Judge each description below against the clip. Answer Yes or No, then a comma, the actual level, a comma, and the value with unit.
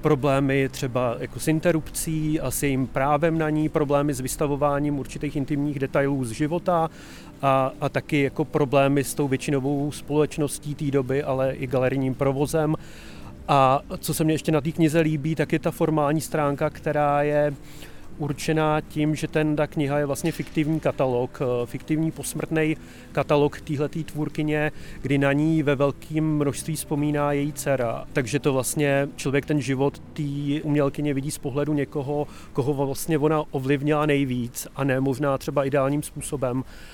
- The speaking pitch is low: No, medium, 145 Hz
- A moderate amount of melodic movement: No, narrow, 1.8 semitones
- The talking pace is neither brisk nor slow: Yes, average, 160 wpm